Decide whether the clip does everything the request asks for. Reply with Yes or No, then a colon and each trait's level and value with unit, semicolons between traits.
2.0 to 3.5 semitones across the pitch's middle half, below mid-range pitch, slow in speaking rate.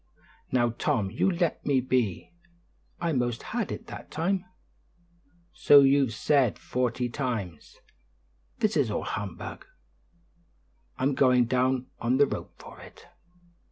Yes: average, 3.2 semitones; low, 130 Hz; slow, 125 wpm